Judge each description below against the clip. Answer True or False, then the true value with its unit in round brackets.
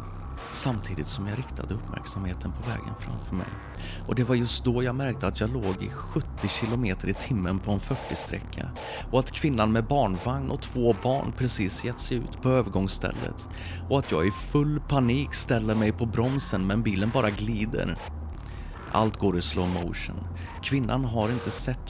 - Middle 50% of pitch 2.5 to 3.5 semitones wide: False (5.1 semitones)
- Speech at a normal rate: True (175 wpm)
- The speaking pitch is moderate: False (105 Hz)